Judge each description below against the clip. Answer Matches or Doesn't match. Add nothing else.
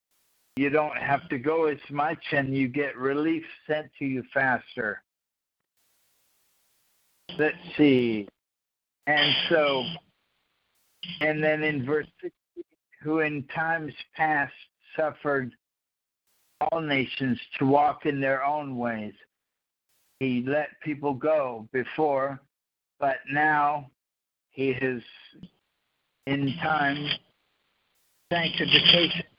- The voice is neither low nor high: Matches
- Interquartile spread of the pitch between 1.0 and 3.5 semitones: Matches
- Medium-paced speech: Doesn't match